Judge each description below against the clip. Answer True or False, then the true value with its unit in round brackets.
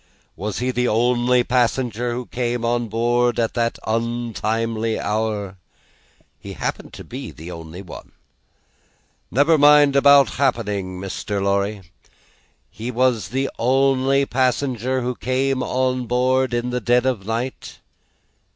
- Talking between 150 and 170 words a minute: False (135 wpm)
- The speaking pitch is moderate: False (120 Hz)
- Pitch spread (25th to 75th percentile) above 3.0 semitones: False (2.6 semitones)